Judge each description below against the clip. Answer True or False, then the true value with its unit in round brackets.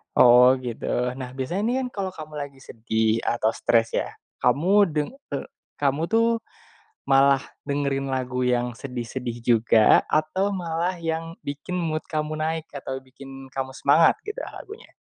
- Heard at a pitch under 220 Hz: True (140 Hz)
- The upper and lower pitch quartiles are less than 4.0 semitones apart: False (4.3 semitones)